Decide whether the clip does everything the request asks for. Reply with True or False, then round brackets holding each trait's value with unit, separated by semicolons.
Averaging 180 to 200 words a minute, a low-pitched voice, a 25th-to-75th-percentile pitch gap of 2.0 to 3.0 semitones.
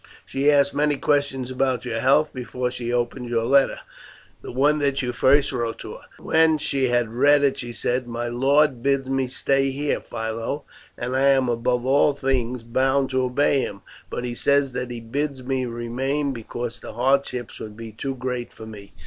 True (190 wpm; 130 Hz; 2.5 semitones)